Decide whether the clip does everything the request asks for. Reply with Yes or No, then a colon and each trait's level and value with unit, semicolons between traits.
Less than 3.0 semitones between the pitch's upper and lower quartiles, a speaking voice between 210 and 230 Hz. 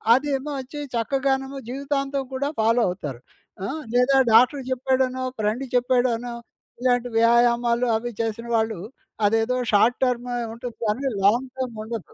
No: narrow, 2.5 semitones; high, 245 Hz